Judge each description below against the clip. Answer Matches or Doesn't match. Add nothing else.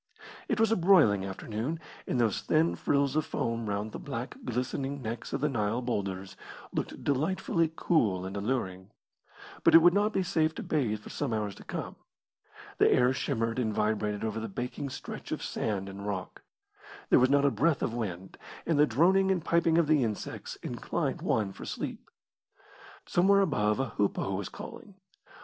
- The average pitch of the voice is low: Matches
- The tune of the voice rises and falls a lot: Matches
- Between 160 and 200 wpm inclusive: Matches